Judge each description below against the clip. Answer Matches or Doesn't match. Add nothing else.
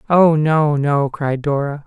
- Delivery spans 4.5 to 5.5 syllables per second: Doesn't match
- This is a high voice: Doesn't match